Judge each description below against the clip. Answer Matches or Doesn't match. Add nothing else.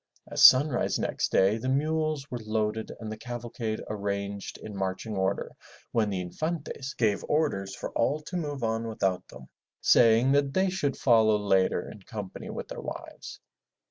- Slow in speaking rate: Doesn't match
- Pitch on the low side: Matches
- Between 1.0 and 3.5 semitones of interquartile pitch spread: Doesn't match